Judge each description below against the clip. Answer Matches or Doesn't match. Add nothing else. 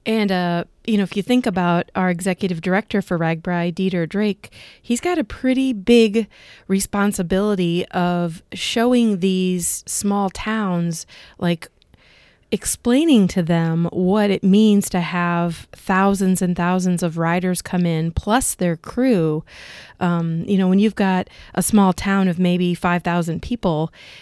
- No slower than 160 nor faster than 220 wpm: Doesn't match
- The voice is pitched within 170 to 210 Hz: Matches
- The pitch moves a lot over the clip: Doesn't match